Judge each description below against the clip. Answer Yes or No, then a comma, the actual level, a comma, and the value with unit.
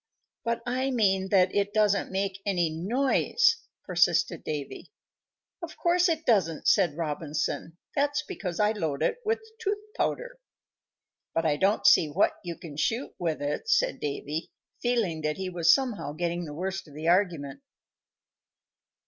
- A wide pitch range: Yes, wide, 6.9 semitones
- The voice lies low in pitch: No, high, 190 Hz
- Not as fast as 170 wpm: Yes, average, 150 wpm